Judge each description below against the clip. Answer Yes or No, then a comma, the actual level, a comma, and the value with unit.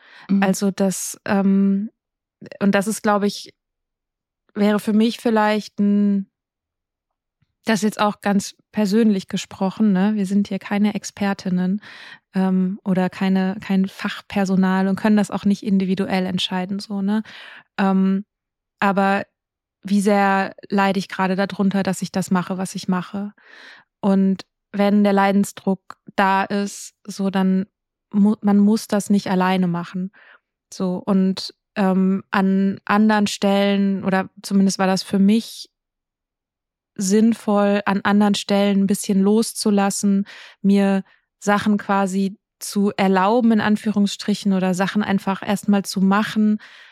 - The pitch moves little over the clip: Yes, narrow, 1.1 semitones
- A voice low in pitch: No, high, 200 Hz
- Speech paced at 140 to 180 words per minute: No, average, 130 wpm